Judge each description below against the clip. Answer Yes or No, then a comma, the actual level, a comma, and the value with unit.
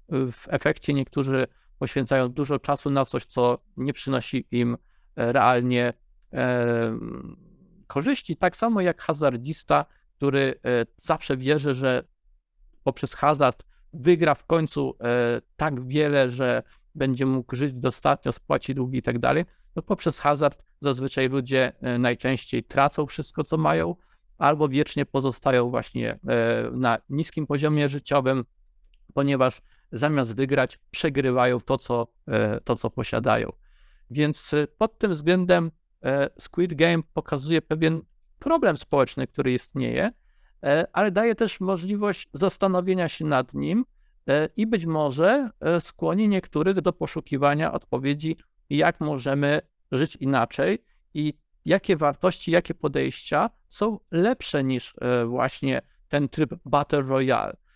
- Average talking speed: Yes, average, 120 wpm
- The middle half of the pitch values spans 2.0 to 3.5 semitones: No, average, 4.0 semitones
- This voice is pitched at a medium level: Yes, medium, 145 Hz